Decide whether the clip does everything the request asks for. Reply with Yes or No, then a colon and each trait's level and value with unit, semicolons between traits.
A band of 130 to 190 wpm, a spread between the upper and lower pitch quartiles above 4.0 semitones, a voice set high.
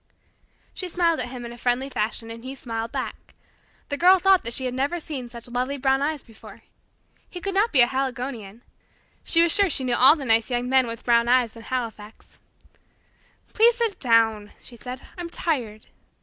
No: average, 200 wpm; average, 4.8 semitones; very high, 255 Hz